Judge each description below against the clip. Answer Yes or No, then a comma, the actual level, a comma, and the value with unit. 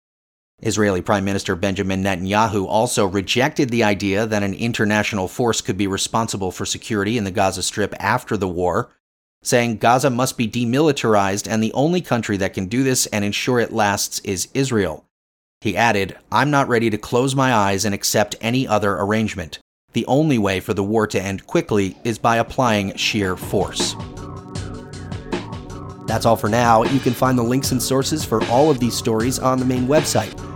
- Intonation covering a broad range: No, average, 3.8 semitones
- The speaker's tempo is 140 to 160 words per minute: No, average, 180 wpm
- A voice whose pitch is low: Yes, low, 110 Hz